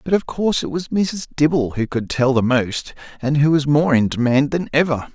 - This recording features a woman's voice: No, male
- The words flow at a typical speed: No, fast, 235 wpm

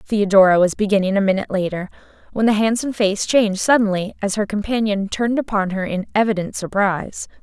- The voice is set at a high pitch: Yes, high, 205 Hz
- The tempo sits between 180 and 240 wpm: No, average, 170 wpm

